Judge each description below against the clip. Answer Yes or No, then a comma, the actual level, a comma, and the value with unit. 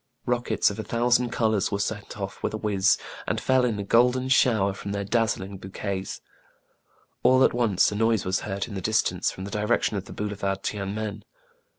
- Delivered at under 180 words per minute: No, fast, 205 wpm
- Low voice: Yes, low, 105 Hz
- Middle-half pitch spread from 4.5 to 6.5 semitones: No, average, 2.8 semitones